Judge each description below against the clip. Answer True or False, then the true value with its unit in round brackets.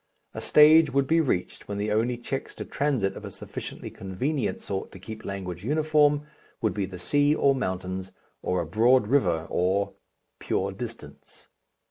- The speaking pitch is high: False (110 Hz)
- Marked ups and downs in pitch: True (6.9 semitones)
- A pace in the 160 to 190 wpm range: True (165 wpm)